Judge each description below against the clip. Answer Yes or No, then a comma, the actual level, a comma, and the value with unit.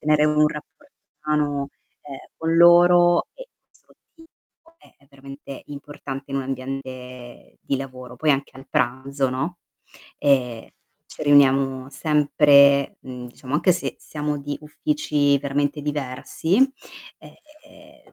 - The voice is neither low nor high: Yes, medium, 145 Hz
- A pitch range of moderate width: No, narrow, 2.1 semitones